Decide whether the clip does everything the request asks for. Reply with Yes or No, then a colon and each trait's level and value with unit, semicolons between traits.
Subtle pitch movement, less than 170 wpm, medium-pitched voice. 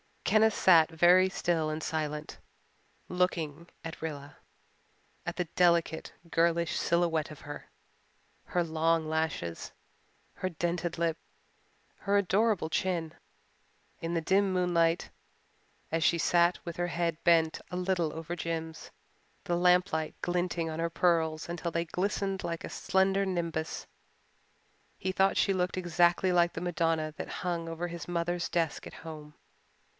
Yes: narrow, 1.8 semitones; average, 140 wpm; medium, 170 Hz